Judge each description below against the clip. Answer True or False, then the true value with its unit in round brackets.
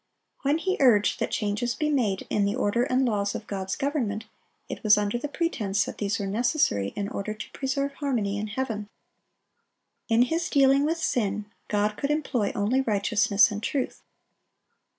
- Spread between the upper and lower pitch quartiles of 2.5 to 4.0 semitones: False (4.9 semitones)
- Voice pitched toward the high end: True (220 Hz)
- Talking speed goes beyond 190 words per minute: False (170 wpm)